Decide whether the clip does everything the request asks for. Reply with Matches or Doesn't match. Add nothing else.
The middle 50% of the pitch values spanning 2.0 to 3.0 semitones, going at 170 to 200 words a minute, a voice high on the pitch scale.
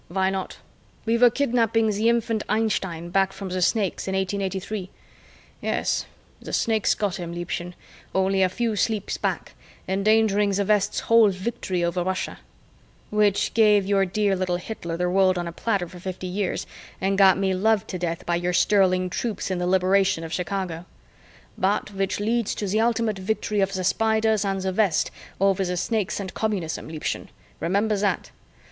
Matches